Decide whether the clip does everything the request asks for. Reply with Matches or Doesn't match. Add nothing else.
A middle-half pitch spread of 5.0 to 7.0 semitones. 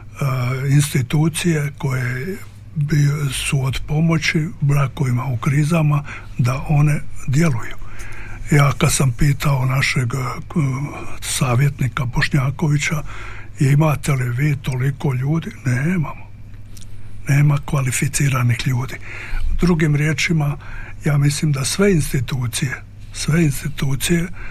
Doesn't match